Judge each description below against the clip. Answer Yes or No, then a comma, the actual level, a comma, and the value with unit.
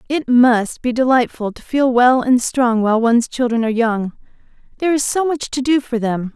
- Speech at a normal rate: No, fast, 210 wpm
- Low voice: No, high, 245 Hz